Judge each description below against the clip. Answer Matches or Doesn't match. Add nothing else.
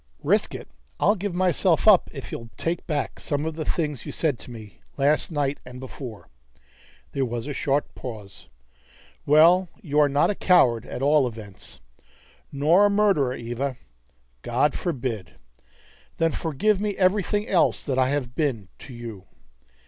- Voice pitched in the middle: Matches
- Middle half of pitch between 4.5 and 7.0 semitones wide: Matches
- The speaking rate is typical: Matches